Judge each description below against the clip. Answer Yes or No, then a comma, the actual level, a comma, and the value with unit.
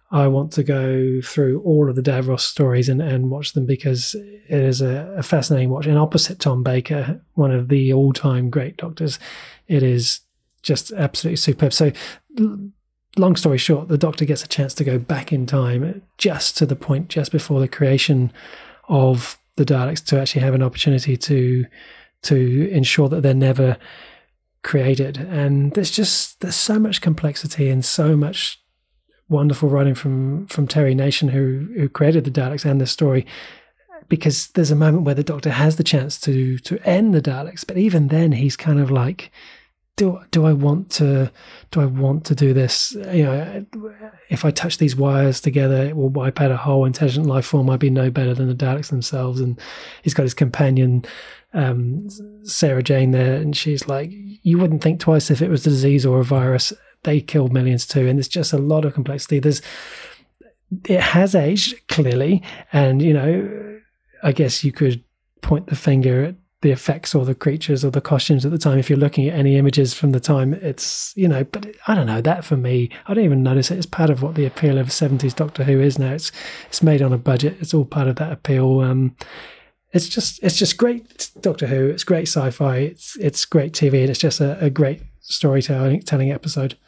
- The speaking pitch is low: No, medium, 145 Hz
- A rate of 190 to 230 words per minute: Yes, average, 200 wpm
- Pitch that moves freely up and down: No, average, 3.1 semitones